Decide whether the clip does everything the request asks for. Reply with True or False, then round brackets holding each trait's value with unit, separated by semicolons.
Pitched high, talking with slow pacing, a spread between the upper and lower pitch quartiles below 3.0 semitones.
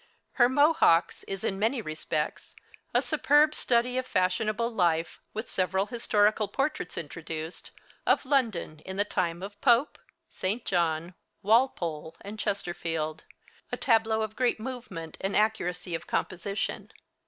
False (200 Hz; 130 wpm; 5.4 semitones)